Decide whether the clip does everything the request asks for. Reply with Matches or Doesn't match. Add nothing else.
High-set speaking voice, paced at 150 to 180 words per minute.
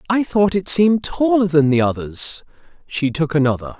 Doesn't match